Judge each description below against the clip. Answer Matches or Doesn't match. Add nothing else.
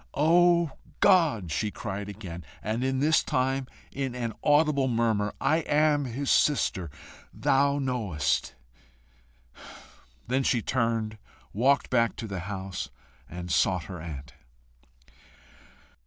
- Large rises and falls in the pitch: Matches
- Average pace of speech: Doesn't match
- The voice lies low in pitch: Matches